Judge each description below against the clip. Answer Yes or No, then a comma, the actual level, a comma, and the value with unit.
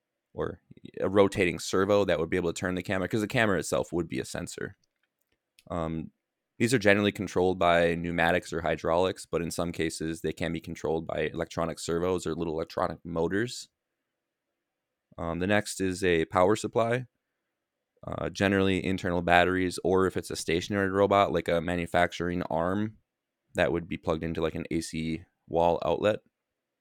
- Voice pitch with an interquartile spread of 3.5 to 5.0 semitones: No, average, 2.9 semitones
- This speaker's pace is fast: No, average, 170 wpm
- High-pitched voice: No, very low, 90 Hz